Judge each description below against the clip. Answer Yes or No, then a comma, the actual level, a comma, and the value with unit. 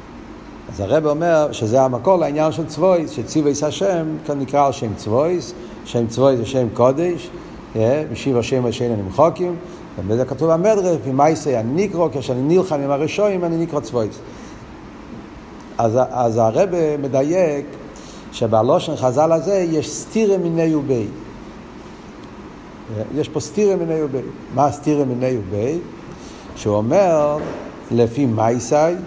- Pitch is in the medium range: Yes, medium, 150 Hz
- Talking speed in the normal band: Yes, average, 130 wpm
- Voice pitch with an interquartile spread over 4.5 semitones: Yes, average, 5.0 semitones